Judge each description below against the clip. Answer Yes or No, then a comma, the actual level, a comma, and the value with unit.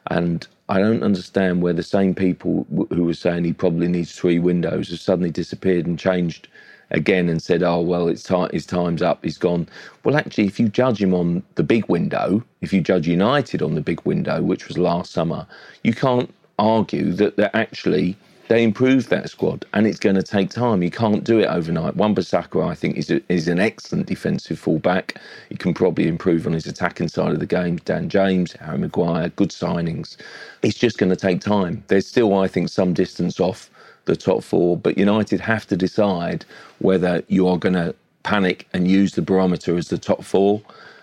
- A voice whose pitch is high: No, very low, 95 Hz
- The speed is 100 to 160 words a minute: No, fast, 205 wpm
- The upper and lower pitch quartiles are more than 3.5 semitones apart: No, narrow, 2.6 semitones